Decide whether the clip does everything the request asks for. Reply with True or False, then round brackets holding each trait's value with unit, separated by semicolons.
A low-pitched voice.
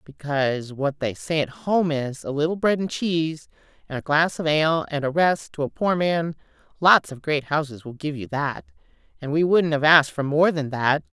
False (155 Hz)